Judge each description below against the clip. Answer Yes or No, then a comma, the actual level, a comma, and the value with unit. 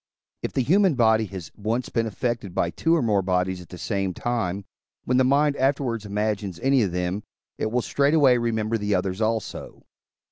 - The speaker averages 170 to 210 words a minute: Yes, average, 185 wpm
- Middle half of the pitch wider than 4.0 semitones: Yes, average, 4.5 semitones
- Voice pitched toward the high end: No, low, 110 Hz